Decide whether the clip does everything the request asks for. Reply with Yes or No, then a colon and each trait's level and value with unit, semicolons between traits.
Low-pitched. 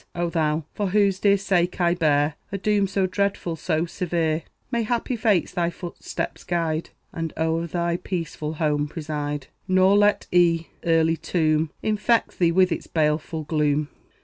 No: medium, 170 Hz